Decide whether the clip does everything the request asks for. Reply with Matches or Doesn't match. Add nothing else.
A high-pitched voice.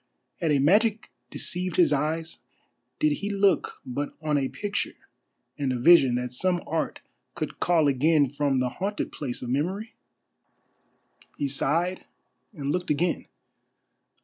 Doesn't match